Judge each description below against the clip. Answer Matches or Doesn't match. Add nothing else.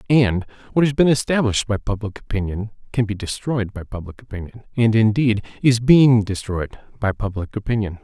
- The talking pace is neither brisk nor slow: Matches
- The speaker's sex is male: Matches